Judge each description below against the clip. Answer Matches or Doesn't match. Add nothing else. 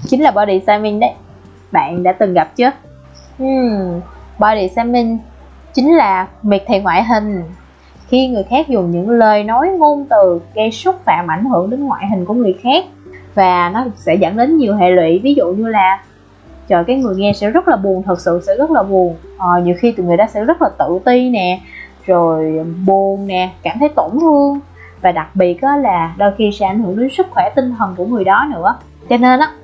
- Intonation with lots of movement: Matches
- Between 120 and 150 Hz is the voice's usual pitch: Doesn't match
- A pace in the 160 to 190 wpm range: Doesn't match